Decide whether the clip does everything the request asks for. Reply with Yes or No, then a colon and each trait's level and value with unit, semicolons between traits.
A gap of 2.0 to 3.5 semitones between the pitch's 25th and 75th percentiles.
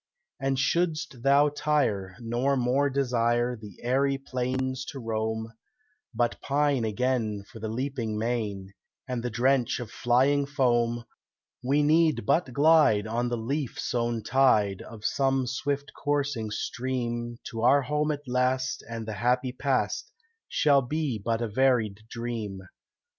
Yes: average, 3.2 semitones